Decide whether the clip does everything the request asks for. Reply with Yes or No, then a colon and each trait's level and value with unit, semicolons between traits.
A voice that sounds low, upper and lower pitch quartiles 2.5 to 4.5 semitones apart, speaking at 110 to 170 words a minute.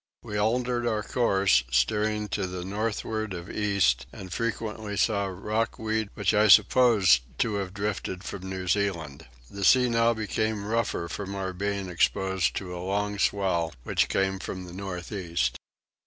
Yes: low, 100 Hz; average, 2.8 semitones; average, 160 wpm